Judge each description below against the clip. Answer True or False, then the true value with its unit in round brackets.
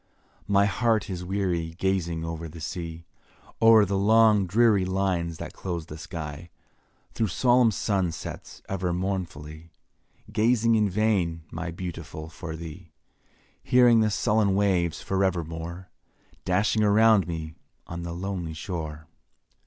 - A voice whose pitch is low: True (90 Hz)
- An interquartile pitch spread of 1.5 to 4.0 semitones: True (3.7 semitones)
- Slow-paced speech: True (130 wpm)